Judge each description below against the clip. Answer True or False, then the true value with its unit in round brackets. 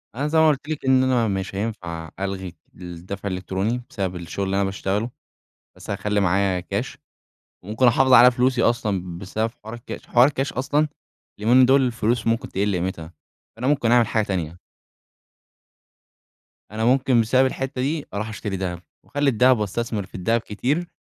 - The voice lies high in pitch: False (110 Hz)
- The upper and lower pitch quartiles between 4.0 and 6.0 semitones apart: True (4.9 semitones)